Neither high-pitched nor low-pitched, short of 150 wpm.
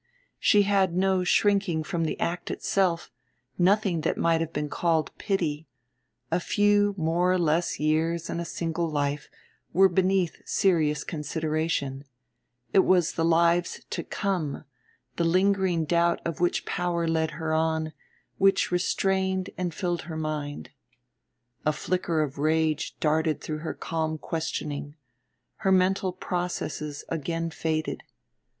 Yes: medium, 165 Hz; slow, 135 wpm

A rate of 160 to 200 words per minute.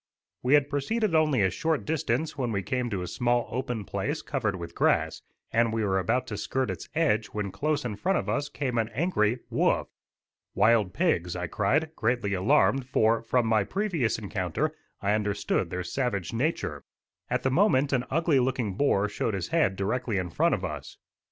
Yes: average, 190 wpm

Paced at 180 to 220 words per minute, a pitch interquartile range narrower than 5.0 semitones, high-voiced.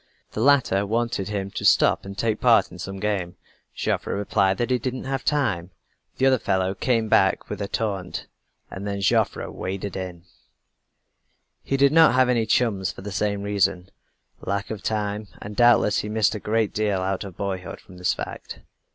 No: average, 185 wpm; average, 2.9 semitones; low, 100 Hz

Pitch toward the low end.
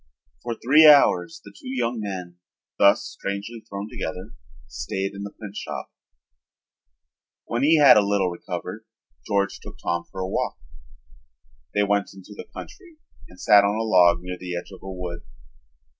Yes: low, 100 Hz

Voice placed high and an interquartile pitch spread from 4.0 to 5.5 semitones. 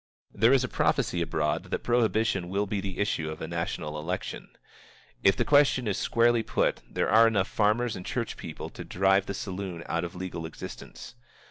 No: very low, 95 Hz; average, 4.5 semitones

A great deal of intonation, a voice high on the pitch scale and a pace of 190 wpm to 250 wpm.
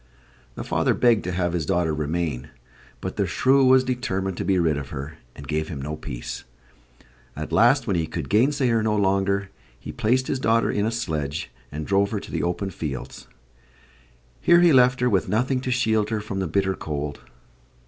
No: wide, 6.9 semitones; very low, 95 Hz; average, 200 wpm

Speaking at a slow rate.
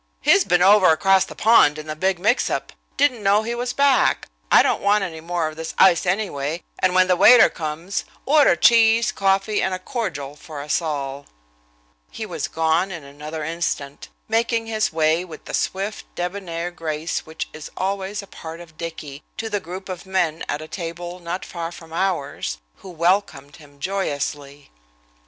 No: average, 180 wpm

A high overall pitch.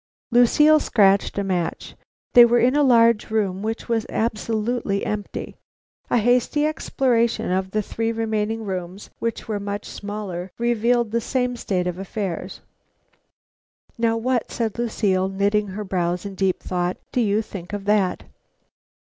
Yes: high, 215 Hz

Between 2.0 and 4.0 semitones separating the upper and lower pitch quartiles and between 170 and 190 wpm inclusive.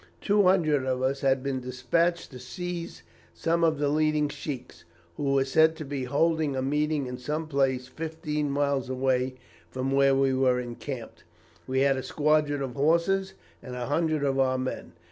Yes: average, 3.0 semitones; average, 180 wpm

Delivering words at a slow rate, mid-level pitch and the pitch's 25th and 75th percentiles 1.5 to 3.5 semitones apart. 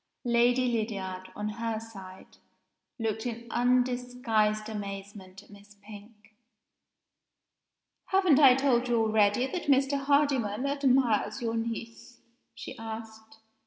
No: slow, 110 wpm; high, 230 Hz; average, 2.9 semitones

